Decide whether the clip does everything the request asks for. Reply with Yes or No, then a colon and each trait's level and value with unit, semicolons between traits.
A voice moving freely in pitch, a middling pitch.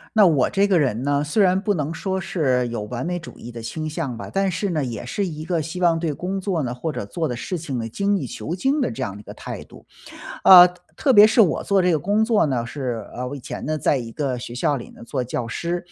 Yes: wide, 6.9 semitones; medium, 155 Hz